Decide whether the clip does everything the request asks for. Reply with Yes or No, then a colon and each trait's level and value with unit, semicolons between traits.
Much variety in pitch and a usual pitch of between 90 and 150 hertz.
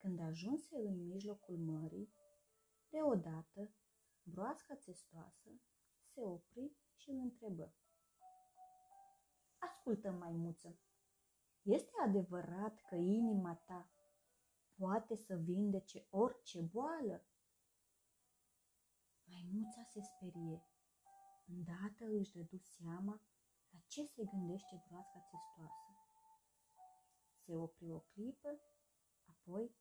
No: wide, 5.8 semitones; high, 195 Hz